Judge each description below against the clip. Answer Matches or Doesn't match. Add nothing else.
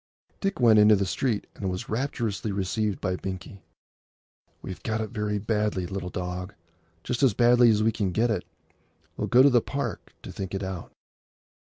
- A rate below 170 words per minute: Doesn't match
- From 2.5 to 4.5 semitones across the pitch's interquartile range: Matches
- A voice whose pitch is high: Doesn't match